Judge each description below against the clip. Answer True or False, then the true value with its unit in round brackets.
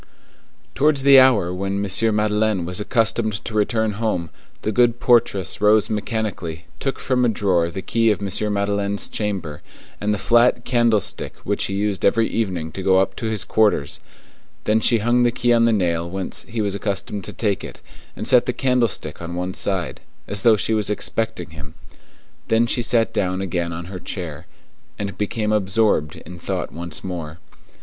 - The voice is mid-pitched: False (105 Hz)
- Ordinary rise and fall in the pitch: True (3.7 semitones)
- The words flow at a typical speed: True (180 wpm)